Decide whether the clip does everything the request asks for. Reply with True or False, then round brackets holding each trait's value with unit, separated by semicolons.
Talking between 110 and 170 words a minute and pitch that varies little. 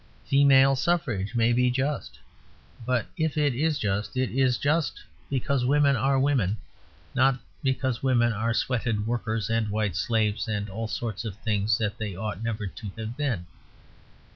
False (160 wpm; 3.8 semitones)